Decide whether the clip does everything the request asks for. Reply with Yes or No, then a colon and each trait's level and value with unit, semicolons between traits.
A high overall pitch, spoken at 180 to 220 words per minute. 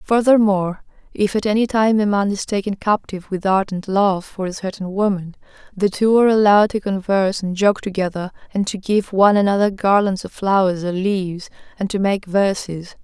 Yes: high, 195 Hz; average, 185 wpm